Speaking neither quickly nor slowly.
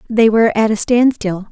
Yes: average, 195 wpm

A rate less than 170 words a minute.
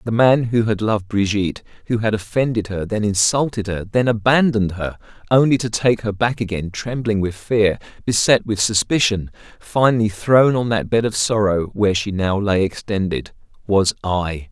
No: average, 175 wpm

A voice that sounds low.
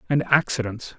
Yes: low, 130 Hz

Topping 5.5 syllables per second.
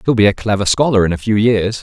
Yes: 6.4 syllables/s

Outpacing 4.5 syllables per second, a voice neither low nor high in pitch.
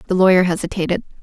Yes: 8.0 syllables/s; medium, 180 Hz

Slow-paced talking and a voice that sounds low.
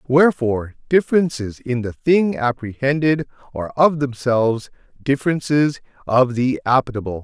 Yes: slow, 110 wpm; low, 130 Hz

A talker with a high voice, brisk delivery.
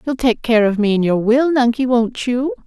Yes: high, 235 Hz; fast, 250 wpm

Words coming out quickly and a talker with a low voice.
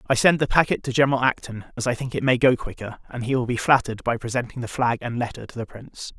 Yes: fast, 270 wpm; low, 120 Hz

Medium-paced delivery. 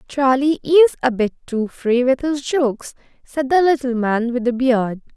Yes: average, 185 wpm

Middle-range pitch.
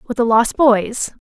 No: high, 235 Hz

